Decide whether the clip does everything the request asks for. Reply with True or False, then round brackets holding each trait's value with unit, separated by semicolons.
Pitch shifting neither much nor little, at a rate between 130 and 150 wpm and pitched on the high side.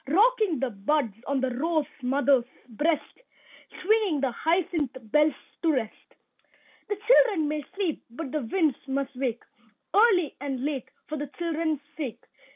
True (4.2 semitones; 145 wpm; 300 Hz)